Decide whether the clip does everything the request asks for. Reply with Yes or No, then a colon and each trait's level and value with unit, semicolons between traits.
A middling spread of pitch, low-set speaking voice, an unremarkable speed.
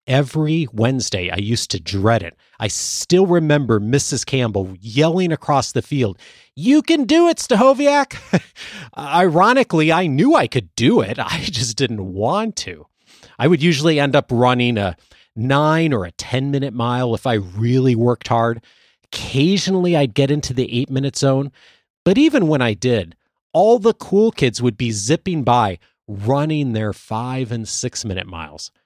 No: wide, 6.0 semitones; low, 130 Hz; average, 165 wpm